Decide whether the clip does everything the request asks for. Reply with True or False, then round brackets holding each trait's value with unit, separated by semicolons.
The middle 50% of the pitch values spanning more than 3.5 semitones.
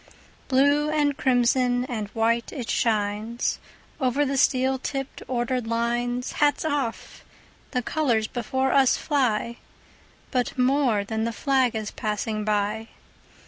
False (3.2 semitones)